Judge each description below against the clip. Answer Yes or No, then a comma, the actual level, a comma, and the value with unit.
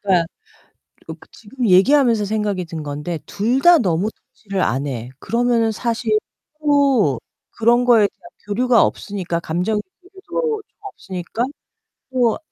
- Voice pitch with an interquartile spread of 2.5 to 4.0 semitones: No, wide, 5.4 semitones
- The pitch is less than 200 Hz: No, high, 215 Hz